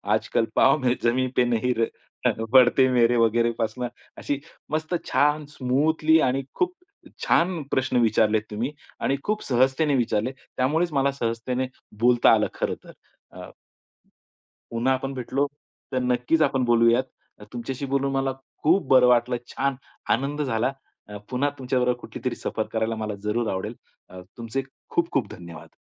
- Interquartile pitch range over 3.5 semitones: No, average, 2.8 semitones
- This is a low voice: Yes, low, 130 Hz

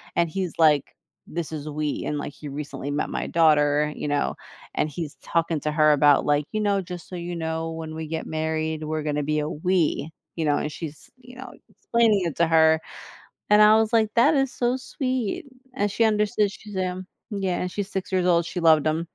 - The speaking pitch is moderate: Yes, medium, 165 Hz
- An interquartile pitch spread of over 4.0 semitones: Yes, average, 4.5 semitones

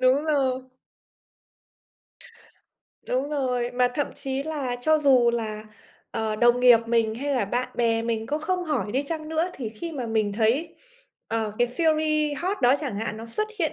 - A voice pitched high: Yes, very high, 255 Hz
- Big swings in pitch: No, average, 4.8 semitones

